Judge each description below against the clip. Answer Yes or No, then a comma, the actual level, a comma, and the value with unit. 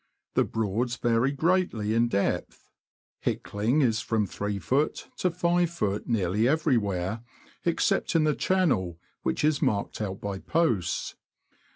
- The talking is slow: Yes, slow, 130 wpm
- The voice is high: No, low, 115 Hz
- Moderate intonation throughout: No, wide, 7.1 semitones